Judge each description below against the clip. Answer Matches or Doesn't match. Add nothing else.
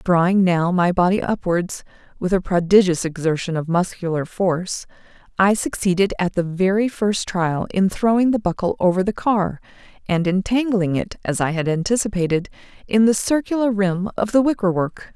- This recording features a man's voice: Doesn't match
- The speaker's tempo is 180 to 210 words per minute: Doesn't match